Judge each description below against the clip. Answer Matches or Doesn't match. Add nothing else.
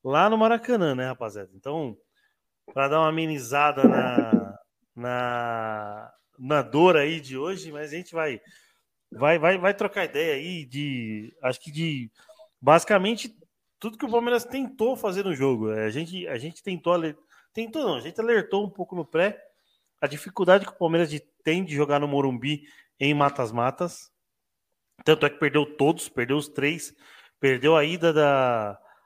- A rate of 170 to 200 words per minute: Doesn't match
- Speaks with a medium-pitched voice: Matches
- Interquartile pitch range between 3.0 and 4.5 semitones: Doesn't match